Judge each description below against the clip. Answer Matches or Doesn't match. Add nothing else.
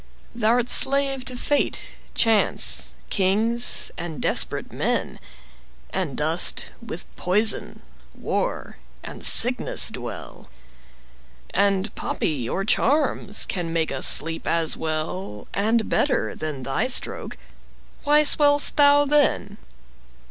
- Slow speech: Matches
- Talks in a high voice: Matches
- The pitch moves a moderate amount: Doesn't match